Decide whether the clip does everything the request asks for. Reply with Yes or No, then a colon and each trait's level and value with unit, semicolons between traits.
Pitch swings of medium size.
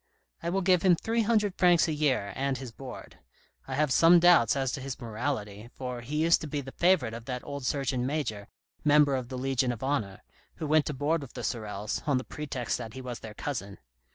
Yes: average, 4.0 semitones